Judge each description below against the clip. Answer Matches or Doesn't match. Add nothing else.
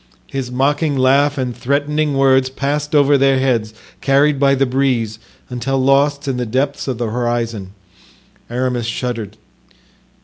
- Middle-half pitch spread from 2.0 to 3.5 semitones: Matches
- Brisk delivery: Doesn't match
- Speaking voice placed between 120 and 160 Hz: Matches